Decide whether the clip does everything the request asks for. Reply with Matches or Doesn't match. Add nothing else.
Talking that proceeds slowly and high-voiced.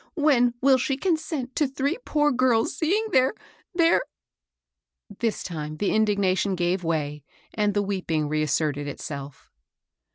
Doesn't match